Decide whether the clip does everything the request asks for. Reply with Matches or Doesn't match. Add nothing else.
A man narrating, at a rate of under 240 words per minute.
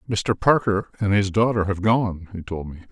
Matches